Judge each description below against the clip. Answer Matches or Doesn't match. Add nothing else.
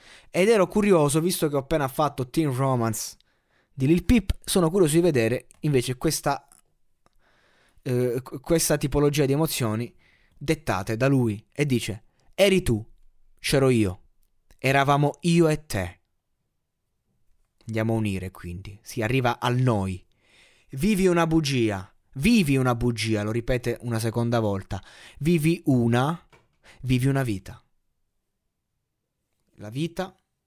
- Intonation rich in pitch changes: Matches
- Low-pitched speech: Matches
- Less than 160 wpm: Matches